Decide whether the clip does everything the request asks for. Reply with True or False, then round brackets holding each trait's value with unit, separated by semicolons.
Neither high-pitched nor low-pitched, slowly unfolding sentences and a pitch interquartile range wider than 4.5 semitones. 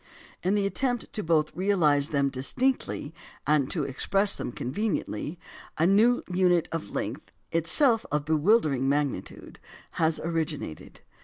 True (165 Hz; 130 wpm; 5.5 semitones)